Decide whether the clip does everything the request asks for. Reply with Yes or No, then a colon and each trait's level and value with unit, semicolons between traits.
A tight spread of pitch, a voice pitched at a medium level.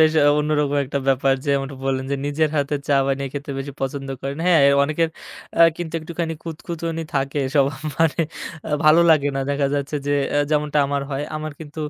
Yes: narrow, 2.2 semitones; medium, 145 Hz